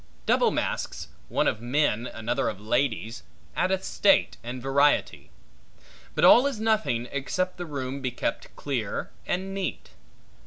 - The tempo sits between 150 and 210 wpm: No, average, 140 wpm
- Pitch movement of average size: No, wide, 7.3 semitones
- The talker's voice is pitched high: No, medium, 140 Hz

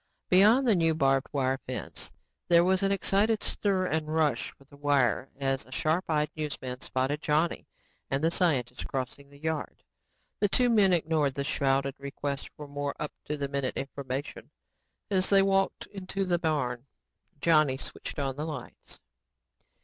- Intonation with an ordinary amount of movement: Yes, average, 4.3 semitones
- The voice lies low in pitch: No, medium, 150 Hz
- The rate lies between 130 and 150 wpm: No, average, 165 wpm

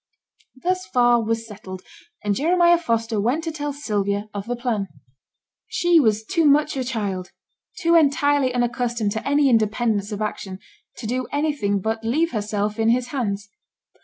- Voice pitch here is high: Yes, high, 235 Hz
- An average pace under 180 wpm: Yes, average, 160 wpm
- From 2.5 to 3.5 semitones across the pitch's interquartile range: No, wide, 5.4 semitones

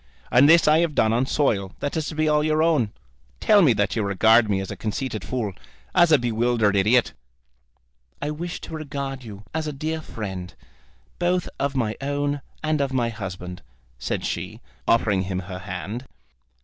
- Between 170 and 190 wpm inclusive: Yes, average, 185 wpm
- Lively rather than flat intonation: Yes, wide, 6.6 semitones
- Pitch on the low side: Yes, low, 125 Hz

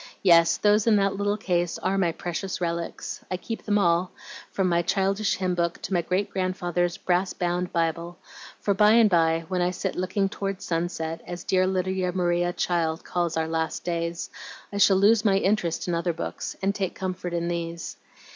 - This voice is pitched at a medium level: Yes, medium, 180 Hz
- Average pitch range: No, narrow, 2.2 semitones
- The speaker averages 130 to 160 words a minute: No, average, 190 wpm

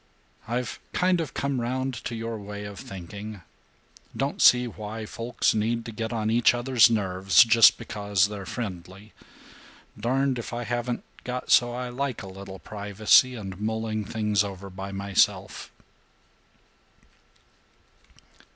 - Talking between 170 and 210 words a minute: No, slow, 135 wpm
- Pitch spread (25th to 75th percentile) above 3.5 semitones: No, average, 3.2 semitones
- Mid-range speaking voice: No, low, 110 Hz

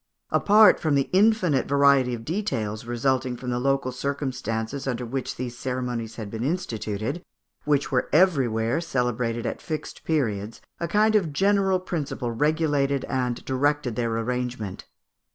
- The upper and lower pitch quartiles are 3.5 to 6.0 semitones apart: Yes, average, 4.2 semitones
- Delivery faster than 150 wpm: No, average, 140 wpm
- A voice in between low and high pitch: No, low, 130 Hz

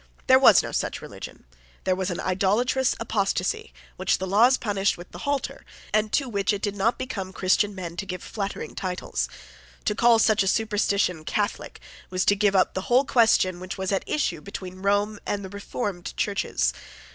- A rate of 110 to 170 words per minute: No, average, 185 wpm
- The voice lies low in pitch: No, high, 200 Hz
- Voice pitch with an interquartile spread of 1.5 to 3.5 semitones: Yes, narrow, 2.5 semitones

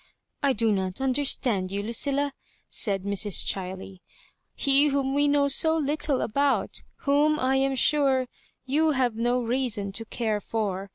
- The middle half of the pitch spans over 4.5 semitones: Yes, average, 5.3 semitones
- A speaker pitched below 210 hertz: No, very high, 255 Hz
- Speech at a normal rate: Yes, average, 160 wpm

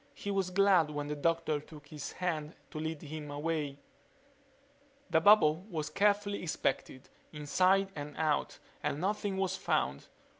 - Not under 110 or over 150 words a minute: Yes, average, 145 wpm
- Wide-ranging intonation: No, average, 4.3 semitones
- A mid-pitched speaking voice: Yes, medium, 160 Hz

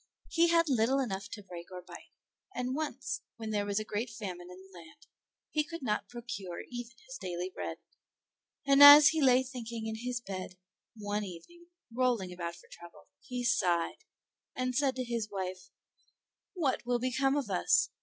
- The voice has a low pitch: No, high, 230 Hz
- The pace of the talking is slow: No, average, 175 wpm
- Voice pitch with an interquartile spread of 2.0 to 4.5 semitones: No, wide, 5.6 semitones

